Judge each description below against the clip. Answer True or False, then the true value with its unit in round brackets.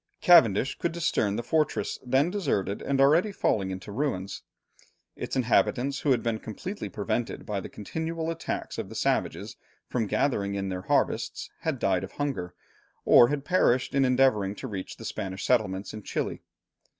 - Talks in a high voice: False (120 Hz)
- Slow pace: False (165 wpm)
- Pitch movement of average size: False (6.4 semitones)